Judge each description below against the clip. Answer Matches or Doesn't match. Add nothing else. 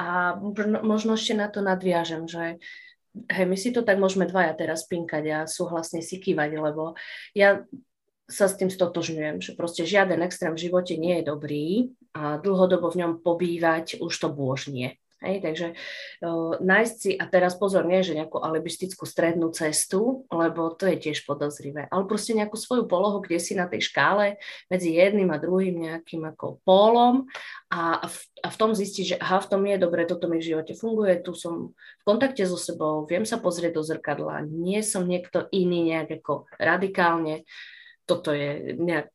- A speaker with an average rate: Doesn't match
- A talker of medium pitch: Matches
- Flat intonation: Doesn't match